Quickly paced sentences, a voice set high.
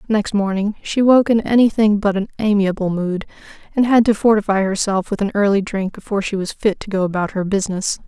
Yes: fast, 210 wpm; high, 205 Hz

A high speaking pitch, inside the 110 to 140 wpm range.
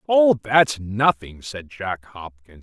No: low, 115 Hz; slow, 135 wpm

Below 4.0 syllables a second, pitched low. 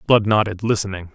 No: 5.9 syllables/s; low, 100 Hz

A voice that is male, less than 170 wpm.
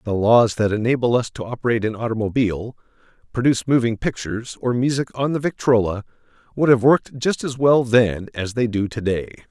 No: male; average, 175 wpm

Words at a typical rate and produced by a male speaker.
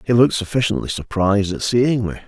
Yes: average, 185 wpm; male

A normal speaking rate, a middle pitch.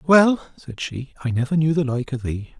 No: fast, 230 wpm; medium, 145 Hz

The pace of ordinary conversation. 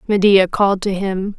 Yes: average, 175 wpm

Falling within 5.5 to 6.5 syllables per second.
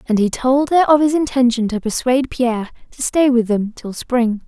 No: 5.2 syllables/s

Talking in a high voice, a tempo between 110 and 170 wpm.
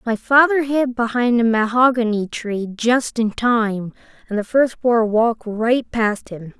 Yes: high, 230 Hz; average, 165 wpm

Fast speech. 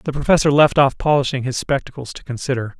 No: average, 195 wpm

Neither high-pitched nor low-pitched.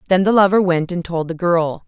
Yes: medium, 180 Hz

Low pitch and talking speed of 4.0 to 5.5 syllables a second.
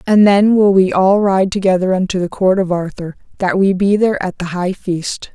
No: high, 190 Hz; 5.0 syllables/s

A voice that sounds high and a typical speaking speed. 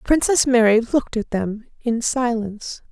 Yes: high, 235 Hz; average, 145 wpm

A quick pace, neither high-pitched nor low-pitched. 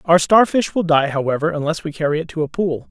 Yes: fast, 250 wpm; medium, 160 Hz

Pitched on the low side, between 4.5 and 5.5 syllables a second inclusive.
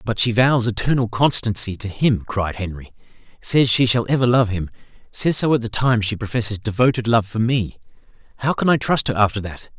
Yes: low, 115 Hz; 5.4 syllables/s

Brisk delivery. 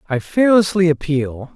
No: slow, 115 wpm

